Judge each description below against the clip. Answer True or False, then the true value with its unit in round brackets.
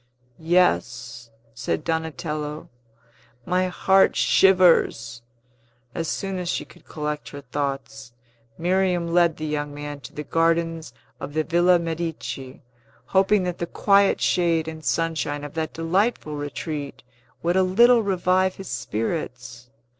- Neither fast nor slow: False (130 wpm)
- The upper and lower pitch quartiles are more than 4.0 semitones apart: False (3.7 semitones)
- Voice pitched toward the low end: False (165 Hz)